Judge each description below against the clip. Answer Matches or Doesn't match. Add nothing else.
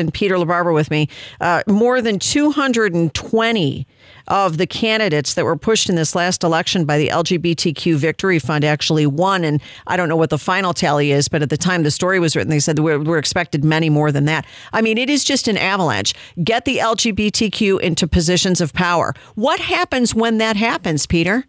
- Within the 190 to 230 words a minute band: Matches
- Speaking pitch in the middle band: Matches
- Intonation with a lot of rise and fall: Matches